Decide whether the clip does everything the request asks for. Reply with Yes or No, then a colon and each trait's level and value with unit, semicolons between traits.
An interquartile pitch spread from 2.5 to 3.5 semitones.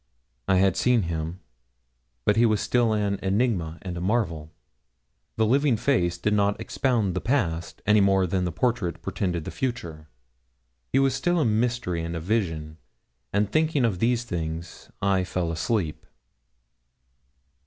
No: wide, 5.5 semitones